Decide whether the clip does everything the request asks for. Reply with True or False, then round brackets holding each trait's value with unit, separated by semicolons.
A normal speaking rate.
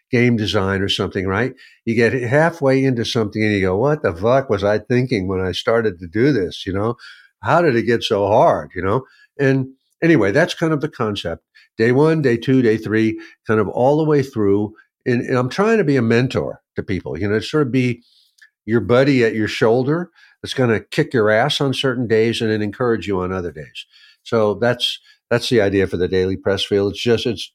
False (225 wpm)